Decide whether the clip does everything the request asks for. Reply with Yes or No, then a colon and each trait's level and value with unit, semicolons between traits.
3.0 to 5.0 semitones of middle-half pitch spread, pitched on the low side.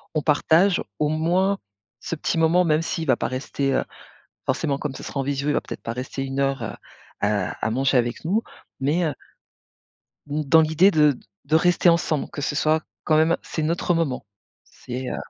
No: average, 3.3 semitones; medium, 150 Hz